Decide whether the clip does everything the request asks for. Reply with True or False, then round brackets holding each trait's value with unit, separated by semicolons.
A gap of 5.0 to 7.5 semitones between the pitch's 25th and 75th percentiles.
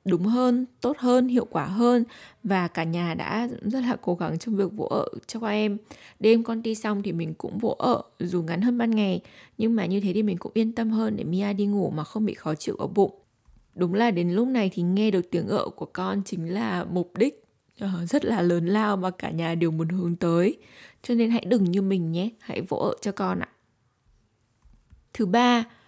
False (4.4 semitones)